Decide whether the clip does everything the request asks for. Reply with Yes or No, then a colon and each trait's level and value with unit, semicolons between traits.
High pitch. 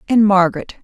Yes: high, 195 Hz